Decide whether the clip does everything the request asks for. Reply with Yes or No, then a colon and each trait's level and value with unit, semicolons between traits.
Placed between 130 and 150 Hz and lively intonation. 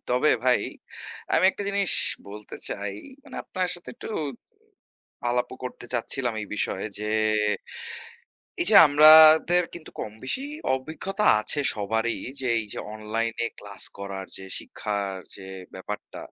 No: low, 120 Hz; wide, 7.0 semitones